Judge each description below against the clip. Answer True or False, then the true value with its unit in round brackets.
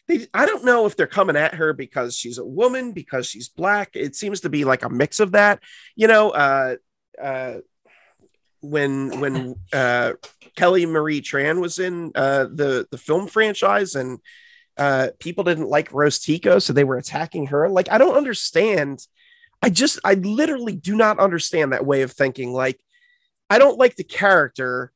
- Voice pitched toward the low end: False (160 Hz)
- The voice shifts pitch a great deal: True (7.8 semitones)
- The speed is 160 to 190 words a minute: True (180 wpm)